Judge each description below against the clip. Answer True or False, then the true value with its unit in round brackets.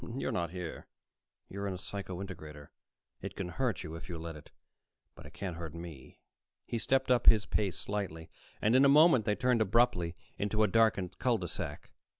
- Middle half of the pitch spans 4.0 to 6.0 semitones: True (5.1 semitones)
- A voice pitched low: True (95 Hz)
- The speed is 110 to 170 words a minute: False (195 wpm)